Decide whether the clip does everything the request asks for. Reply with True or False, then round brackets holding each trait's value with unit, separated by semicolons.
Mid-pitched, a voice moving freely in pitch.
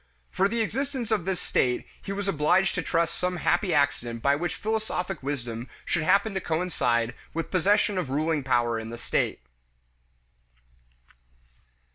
True (175 Hz; 6.4 semitones)